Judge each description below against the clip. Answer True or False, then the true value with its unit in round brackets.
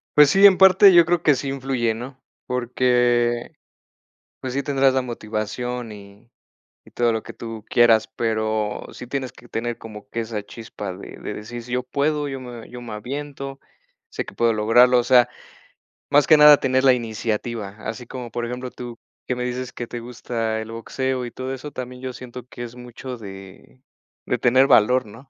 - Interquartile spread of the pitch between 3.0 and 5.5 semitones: False (2.4 semitones)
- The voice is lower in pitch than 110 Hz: False (125 Hz)